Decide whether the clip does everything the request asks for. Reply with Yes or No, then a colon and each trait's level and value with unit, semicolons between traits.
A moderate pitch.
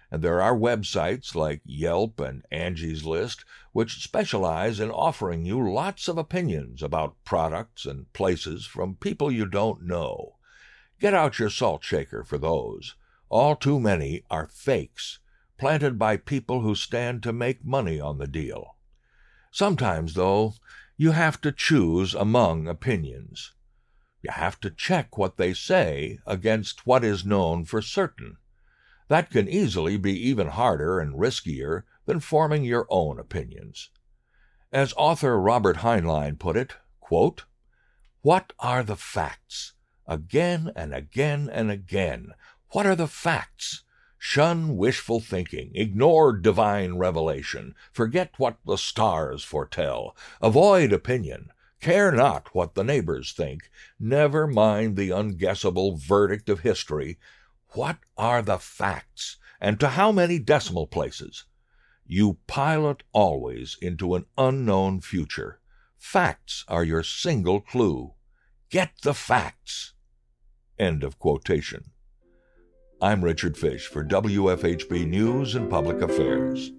No: low, 105 Hz